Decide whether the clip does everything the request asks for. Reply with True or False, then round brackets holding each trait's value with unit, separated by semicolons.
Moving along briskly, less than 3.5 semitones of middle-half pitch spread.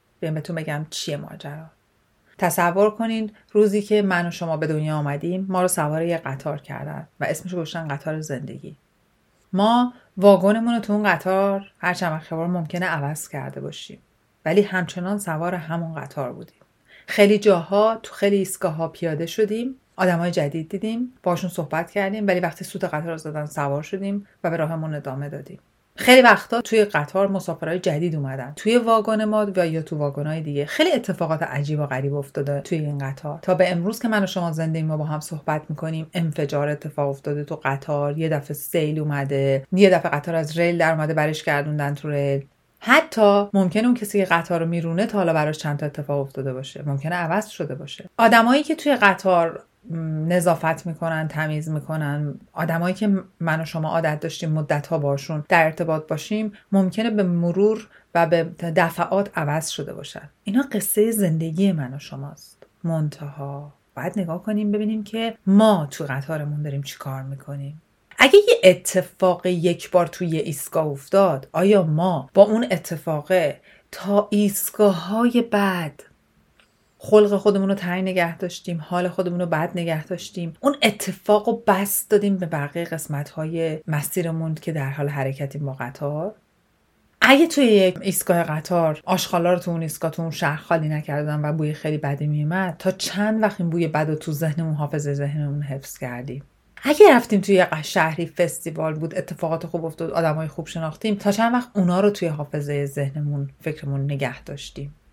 False (170 wpm; 4.3 semitones)